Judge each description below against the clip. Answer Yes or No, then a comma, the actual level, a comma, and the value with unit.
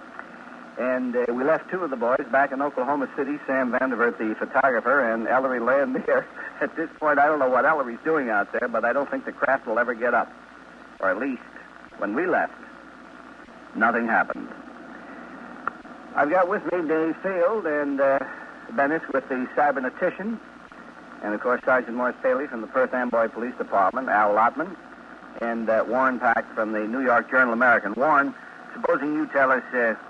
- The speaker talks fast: No, average, 180 wpm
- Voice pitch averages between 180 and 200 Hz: No, medium, 140 Hz